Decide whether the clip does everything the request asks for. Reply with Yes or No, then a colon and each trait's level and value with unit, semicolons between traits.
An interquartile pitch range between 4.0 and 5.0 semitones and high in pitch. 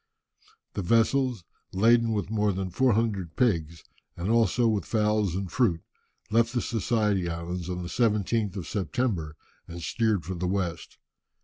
No: average, 4.4 semitones; low, 100 Hz